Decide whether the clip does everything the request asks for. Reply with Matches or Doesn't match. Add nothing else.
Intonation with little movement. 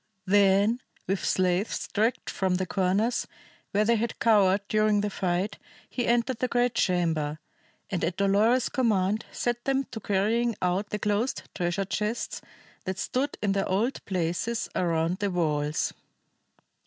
Doesn't match